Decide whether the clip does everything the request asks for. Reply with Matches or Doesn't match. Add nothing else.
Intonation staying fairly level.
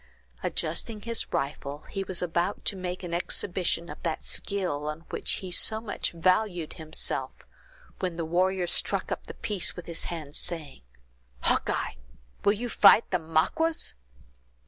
Doesn't match